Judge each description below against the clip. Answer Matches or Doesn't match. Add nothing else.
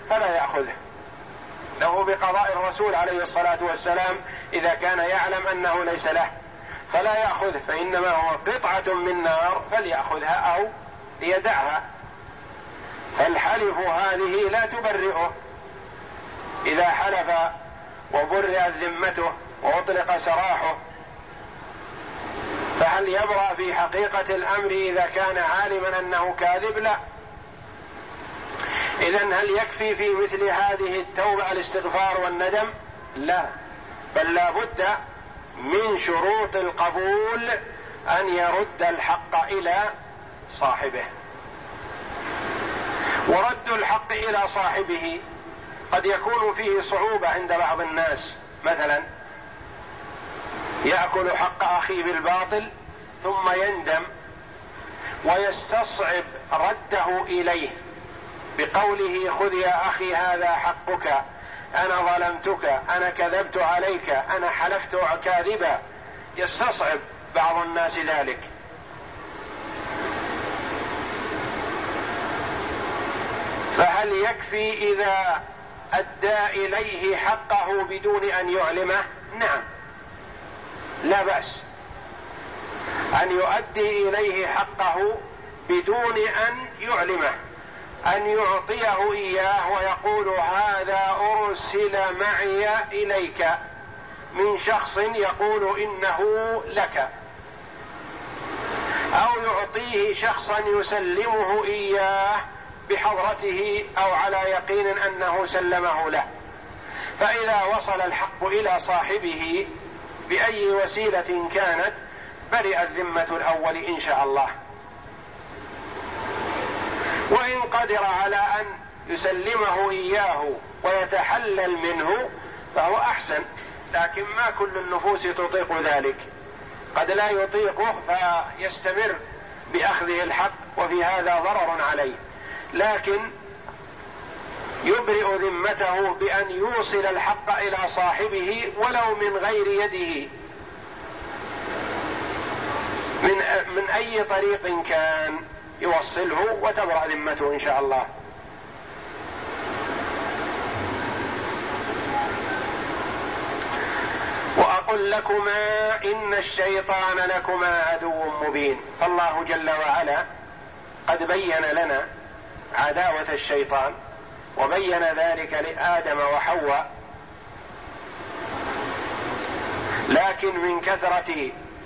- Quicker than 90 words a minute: Doesn't match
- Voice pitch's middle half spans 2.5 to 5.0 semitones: Matches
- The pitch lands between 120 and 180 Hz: Doesn't match